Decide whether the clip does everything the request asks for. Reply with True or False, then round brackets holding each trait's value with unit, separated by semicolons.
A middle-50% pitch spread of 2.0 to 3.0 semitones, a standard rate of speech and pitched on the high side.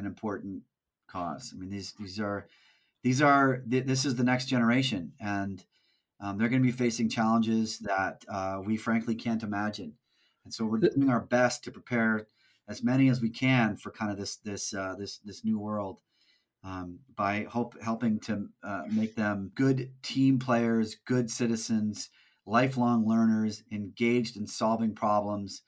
False (2.7 semitones; 165 wpm; 110 Hz)